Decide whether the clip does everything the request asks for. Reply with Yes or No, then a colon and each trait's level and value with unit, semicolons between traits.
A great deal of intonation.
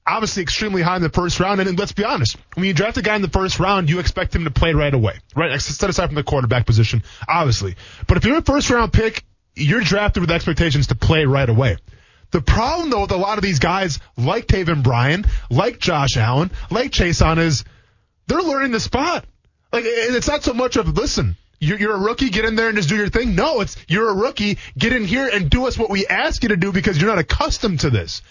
Yes: wide, 8.4 semitones